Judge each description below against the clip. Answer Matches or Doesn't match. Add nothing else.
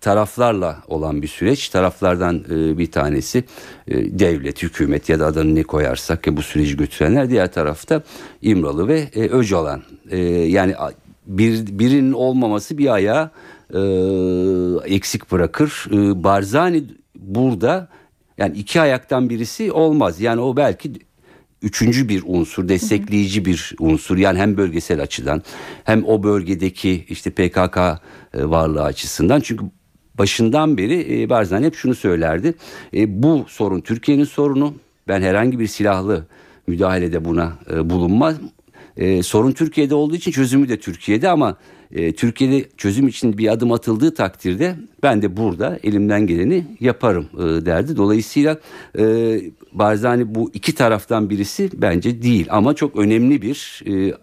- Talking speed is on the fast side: Doesn't match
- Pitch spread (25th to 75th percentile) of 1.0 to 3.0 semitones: Doesn't match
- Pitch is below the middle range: Matches